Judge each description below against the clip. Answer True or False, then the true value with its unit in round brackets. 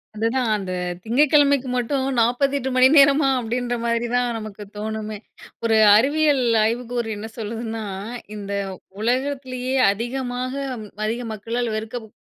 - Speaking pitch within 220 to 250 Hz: True (245 Hz)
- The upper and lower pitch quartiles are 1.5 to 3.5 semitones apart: True (2.9 semitones)